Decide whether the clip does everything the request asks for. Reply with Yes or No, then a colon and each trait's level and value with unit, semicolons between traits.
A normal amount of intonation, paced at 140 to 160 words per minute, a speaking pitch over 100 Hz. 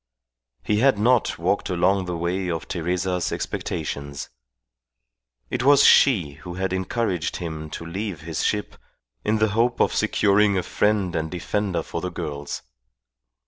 No: average, 3.8 semitones; average, 145 wpm; very low, 90 Hz